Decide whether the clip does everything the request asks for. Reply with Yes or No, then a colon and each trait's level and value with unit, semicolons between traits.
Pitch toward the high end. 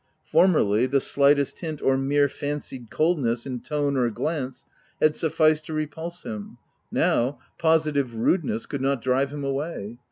No: medium, 140 Hz